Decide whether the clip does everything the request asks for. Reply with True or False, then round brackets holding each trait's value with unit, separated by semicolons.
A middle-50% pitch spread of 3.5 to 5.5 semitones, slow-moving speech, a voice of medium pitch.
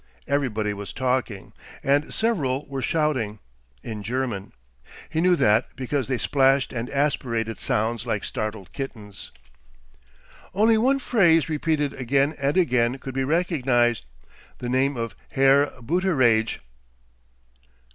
False (4.2 semitones; 120 wpm; 130 Hz)